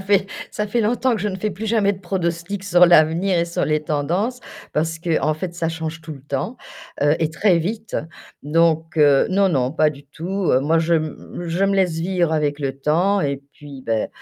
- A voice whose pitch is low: No, medium, 165 Hz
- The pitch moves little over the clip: No, average, 4.1 semitones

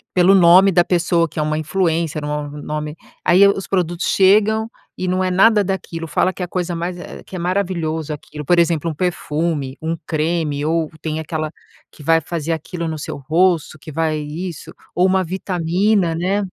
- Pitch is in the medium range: Yes, medium, 170 Hz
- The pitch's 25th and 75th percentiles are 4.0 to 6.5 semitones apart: No, average, 2.8 semitones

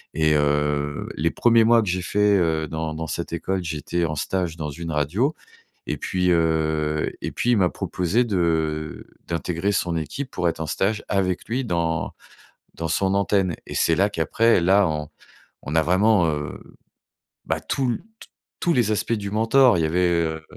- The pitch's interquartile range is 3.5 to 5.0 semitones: Yes, average, 4.4 semitones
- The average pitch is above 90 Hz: No, very low, 85 Hz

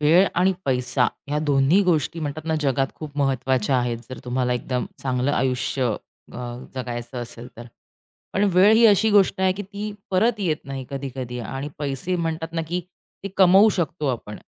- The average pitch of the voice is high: No, medium, 140 Hz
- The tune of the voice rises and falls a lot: Yes, wide, 5.9 semitones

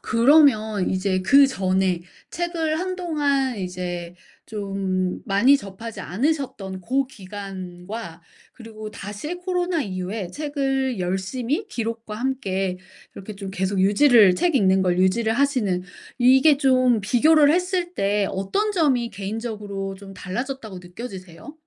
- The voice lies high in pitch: Yes, high, 220 Hz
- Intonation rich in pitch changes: Yes, wide, 6.3 semitones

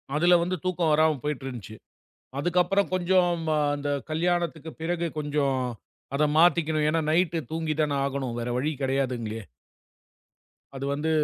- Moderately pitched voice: Yes, medium, 155 Hz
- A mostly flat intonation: No, average, 3.7 semitones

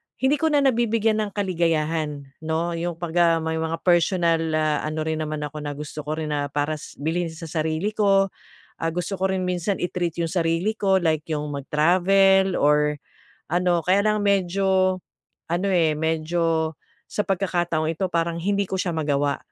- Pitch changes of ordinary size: Yes, average, 3.4 semitones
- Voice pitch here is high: No, medium, 170 Hz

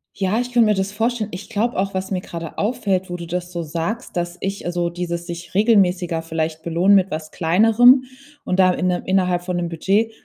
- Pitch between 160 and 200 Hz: Yes, medium, 185 Hz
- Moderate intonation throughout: Yes, average, 3.0 semitones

